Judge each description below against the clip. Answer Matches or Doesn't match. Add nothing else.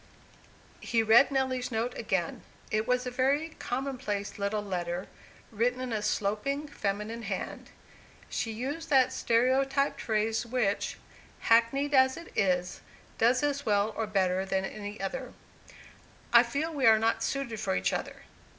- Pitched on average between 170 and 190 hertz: Doesn't match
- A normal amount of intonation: Matches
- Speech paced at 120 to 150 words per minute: Matches